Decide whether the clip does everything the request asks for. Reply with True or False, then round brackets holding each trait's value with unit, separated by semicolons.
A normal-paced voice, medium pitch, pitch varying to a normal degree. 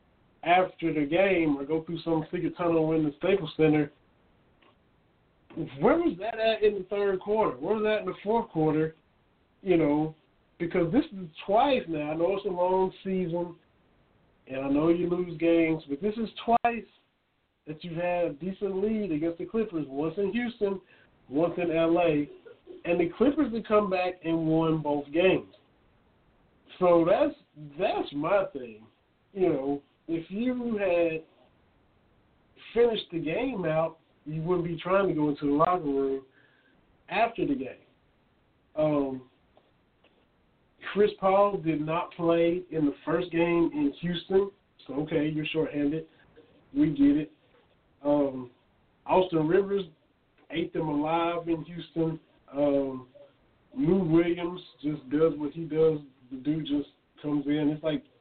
True (150 wpm; 165 Hz; 4.1 semitones)